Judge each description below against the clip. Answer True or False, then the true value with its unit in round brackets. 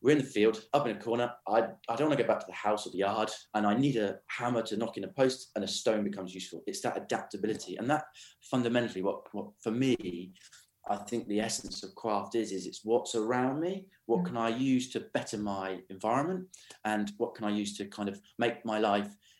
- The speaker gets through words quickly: True (240 wpm)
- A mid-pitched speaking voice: False (110 Hz)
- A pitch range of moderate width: True (3.3 semitones)